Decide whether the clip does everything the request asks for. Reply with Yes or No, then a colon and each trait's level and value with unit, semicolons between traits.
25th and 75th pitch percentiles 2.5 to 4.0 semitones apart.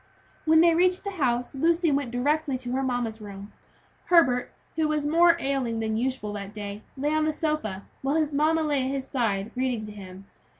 No: wide, 5.6 semitones